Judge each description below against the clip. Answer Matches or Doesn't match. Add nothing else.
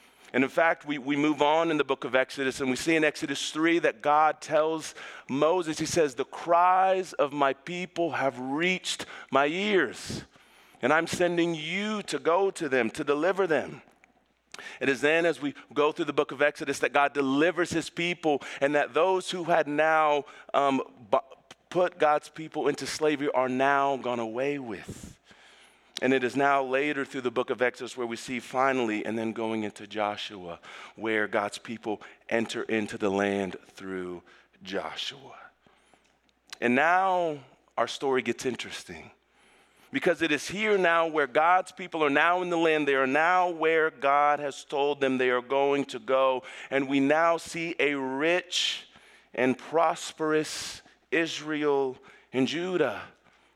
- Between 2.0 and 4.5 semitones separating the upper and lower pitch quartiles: Matches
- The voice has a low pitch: Doesn't match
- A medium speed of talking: Matches